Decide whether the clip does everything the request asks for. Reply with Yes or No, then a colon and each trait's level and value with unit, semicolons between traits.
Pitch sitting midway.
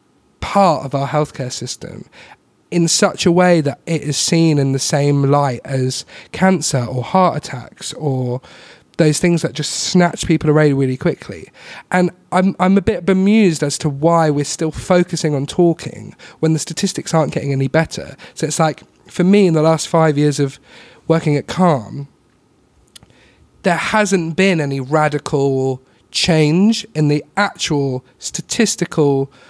Yes: medium, 155 Hz